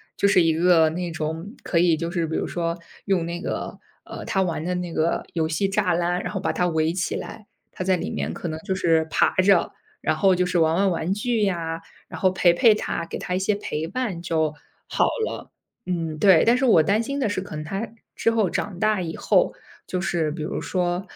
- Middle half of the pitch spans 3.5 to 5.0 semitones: No, average, 3.0 semitones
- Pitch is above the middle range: No, medium, 175 Hz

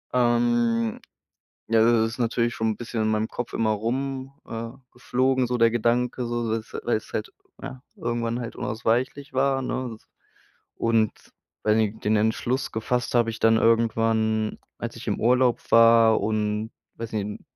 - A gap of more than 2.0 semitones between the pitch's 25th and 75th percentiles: No, narrow, 1.6 semitones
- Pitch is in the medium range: No, low, 115 Hz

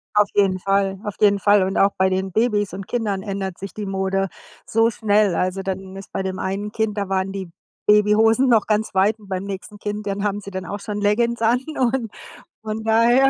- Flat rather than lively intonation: Yes, narrow, 2.0 semitones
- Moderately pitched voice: No, high, 205 Hz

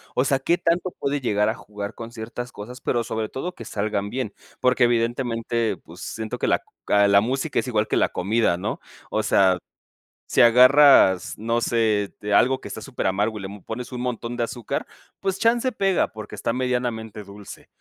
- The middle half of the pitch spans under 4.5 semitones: Yes, average, 3.4 semitones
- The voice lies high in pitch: No, low, 115 Hz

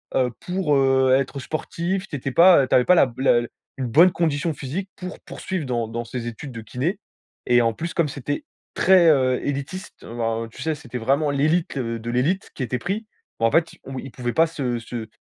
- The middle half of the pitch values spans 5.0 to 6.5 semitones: Yes, wide, 5.4 semitones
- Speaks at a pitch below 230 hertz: Yes, low, 135 Hz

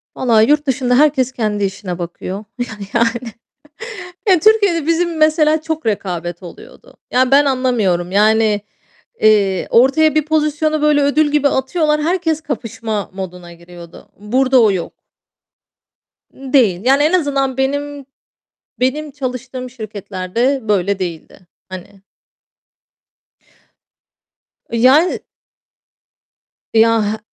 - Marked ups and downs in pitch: Yes, wide, 6.5 semitones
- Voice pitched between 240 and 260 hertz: Yes, very high, 255 Hz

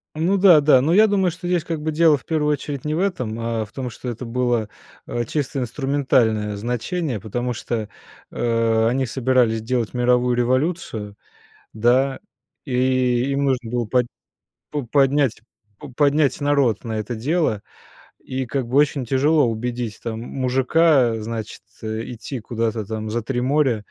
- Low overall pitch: Yes, low, 125 Hz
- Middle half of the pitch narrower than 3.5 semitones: No, average, 3.8 semitones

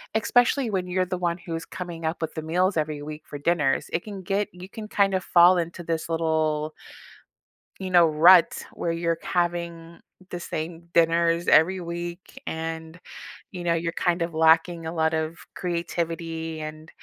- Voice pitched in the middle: Yes, medium, 170 Hz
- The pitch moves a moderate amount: No, narrow, 1.7 semitones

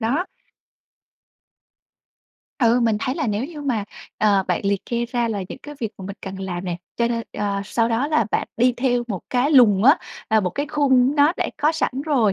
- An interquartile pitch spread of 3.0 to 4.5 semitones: No, average, 5.0 semitones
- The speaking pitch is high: Yes, high, 235 Hz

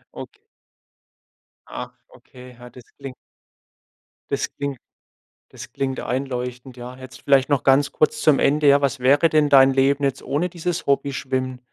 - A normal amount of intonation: No, narrow, 1.8 semitones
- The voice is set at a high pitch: No, low, 135 Hz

